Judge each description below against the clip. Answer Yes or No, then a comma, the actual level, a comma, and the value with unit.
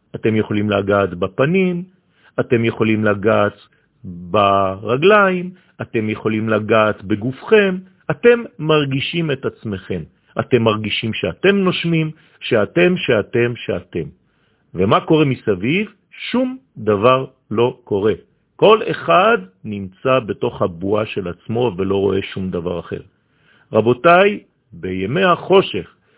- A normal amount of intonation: No, wide, 8.4 semitones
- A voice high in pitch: No, low, 120 Hz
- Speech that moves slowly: Yes, slow, 105 wpm